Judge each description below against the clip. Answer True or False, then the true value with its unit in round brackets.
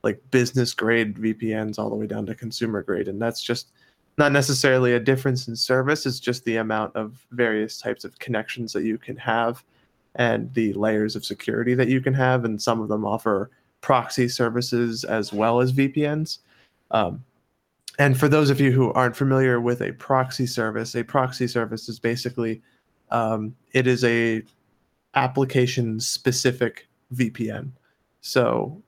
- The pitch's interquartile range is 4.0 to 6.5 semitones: False (2.6 semitones)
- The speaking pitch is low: True (120 Hz)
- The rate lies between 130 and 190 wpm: True (165 wpm)